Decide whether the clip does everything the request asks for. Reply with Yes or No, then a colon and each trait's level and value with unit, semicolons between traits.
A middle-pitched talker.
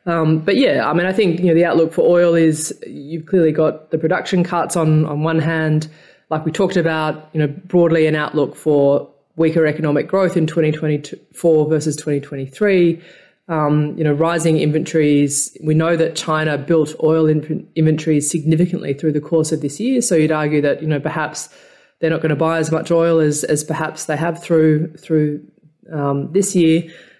Yes: medium, 160 Hz